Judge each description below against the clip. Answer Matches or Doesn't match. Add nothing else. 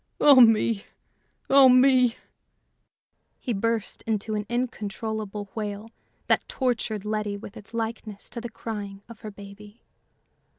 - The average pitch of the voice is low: Doesn't match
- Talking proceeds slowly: Matches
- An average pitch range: Doesn't match